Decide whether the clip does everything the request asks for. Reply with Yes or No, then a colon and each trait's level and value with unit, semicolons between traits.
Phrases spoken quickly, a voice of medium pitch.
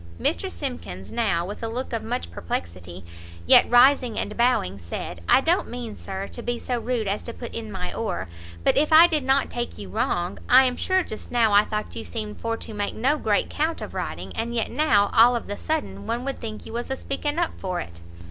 No: fast, 225 wpm; high, 230 Hz